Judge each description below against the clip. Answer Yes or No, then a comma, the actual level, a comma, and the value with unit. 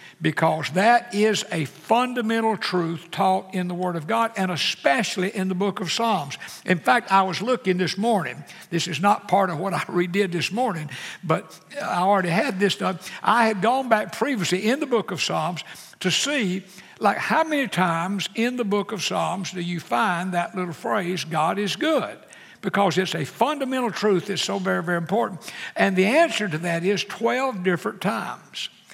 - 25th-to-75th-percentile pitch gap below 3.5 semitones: No, average, 4.1 semitones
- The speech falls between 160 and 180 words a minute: No, average, 190 wpm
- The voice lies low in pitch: No, high, 190 Hz